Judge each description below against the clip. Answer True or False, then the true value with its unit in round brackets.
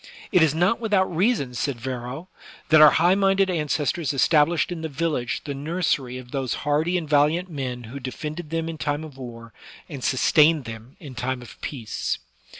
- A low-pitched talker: False (150 Hz)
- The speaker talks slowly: False (180 wpm)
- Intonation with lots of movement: False (4.5 semitones)